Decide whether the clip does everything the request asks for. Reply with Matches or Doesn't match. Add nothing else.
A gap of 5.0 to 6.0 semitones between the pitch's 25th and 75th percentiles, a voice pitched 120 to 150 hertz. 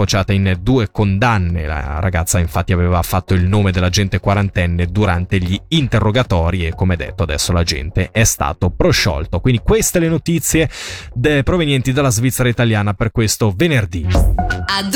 Doesn't match